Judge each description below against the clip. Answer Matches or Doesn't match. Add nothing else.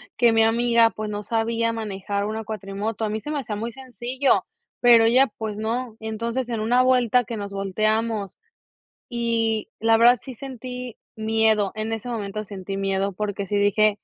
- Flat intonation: Matches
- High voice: Matches